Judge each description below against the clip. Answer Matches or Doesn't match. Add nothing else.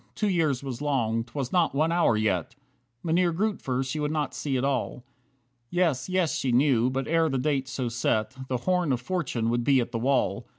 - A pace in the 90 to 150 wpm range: Doesn't match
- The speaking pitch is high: Doesn't match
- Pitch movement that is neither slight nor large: Matches